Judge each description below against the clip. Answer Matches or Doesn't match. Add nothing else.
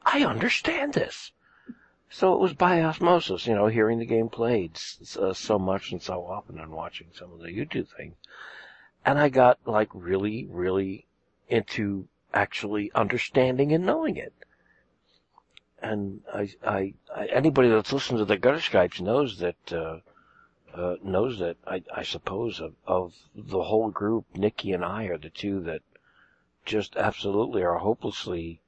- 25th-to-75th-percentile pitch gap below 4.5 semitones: Doesn't match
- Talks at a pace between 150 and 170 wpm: Matches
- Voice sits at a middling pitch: Doesn't match